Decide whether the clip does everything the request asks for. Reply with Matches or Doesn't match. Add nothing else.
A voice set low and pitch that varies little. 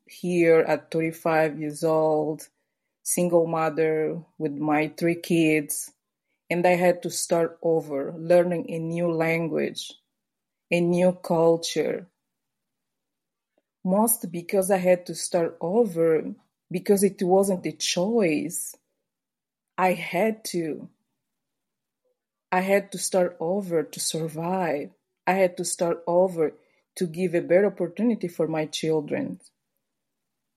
Doesn't match